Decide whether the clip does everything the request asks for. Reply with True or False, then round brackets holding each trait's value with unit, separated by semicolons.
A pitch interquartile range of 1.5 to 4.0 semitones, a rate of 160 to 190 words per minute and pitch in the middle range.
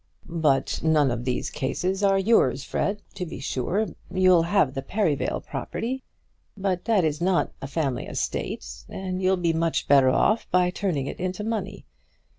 False (5.2 semitones; 165 wpm; 180 Hz)